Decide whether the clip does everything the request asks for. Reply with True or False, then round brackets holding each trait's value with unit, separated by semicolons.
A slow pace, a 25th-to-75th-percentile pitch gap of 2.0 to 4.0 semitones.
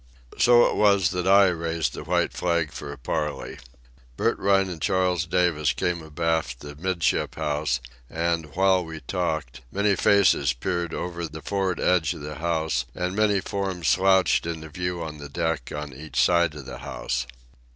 False (170 wpm; 3.4 semitones)